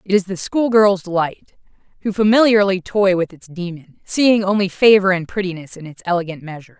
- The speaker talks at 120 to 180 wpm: Yes, average, 175 wpm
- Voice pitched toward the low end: No, high, 190 Hz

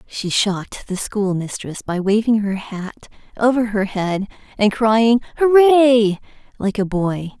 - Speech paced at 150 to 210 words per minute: No, average, 140 wpm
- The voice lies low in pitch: No, high, 215 Hz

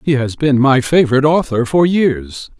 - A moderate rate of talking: Yes, average, 185 wpm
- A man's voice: Yes, male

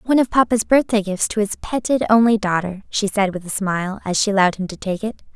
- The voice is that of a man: No, female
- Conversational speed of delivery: No, fast, 245 wpm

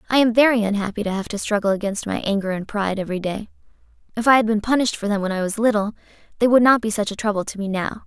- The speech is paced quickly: Yes, fast, 270 wpm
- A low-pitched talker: No, high, 210 Hz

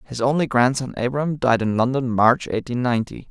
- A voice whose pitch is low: Yes, low, 125 Hz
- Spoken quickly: No, average, 180 wpm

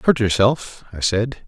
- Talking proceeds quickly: No, average, 160 wpm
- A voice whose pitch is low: Yes, low, 115 Hz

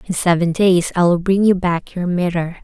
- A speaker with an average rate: No, fast, 230 wpm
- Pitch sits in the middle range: Yes, medium, 180 Hz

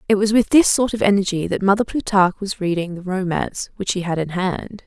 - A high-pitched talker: Yes, high, 195 Hz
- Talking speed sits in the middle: No, fast, 235 wpm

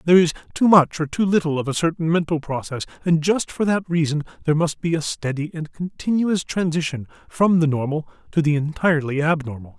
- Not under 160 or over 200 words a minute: Yes, average, 195 wpm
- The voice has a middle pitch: Yes, medium, 160 Hz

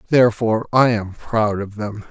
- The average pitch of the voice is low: Yes, low, 110 Hz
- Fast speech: No, average, 170 wpm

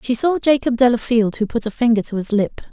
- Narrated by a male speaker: No, female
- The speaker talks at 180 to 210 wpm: No, fast, 245 wpm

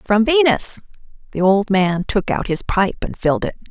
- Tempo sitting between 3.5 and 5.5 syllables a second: Yes, 4.9 syllables/s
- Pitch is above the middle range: Yes, high, 205 Hz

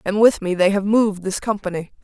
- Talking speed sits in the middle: No, fast, 235 wpm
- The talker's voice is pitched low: No, high, 200 Hz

